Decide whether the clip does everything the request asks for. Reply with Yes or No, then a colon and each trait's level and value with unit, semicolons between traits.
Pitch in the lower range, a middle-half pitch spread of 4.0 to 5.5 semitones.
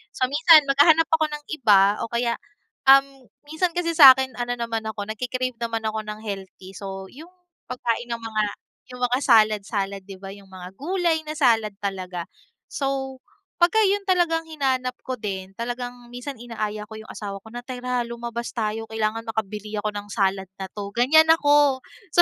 No: high, 235 Hz; average, 4.5 semitones